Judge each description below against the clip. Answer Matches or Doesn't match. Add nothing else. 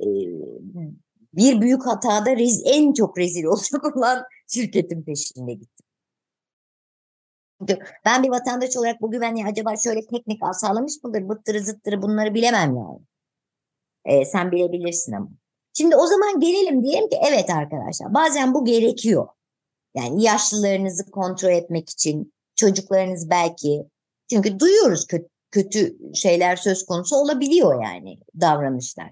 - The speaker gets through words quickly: Doesn't match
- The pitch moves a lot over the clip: Matches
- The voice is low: Doesn't match